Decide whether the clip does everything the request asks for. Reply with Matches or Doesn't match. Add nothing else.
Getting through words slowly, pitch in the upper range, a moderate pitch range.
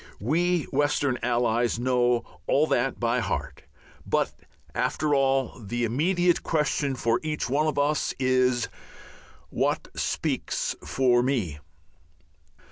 Doesn't match